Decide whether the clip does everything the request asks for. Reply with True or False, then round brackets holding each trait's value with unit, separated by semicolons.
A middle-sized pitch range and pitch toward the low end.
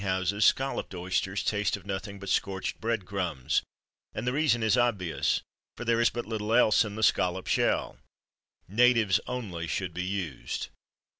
True (3.8 semitones; 100 Hz)